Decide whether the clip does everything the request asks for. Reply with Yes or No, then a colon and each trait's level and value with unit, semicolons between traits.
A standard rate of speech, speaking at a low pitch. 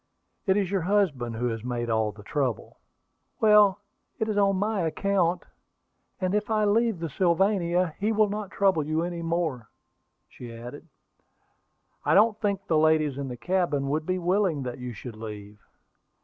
No: average, 170 wpm; medium, 170 Hz